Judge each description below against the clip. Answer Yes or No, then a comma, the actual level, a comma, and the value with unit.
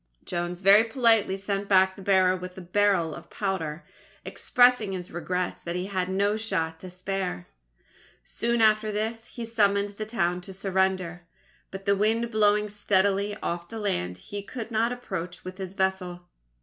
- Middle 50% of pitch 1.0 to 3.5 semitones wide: Yes, average, 2.7 semitones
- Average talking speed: Yes, average, 165 wpm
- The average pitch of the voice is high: Yes, high, 195 Hz